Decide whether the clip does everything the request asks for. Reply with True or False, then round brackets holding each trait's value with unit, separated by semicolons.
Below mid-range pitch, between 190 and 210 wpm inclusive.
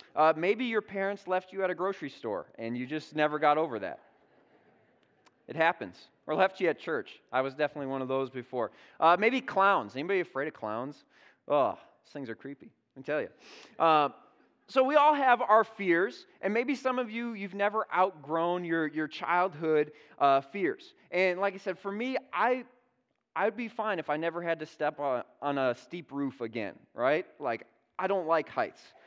False (180 Hz; 195 wpm)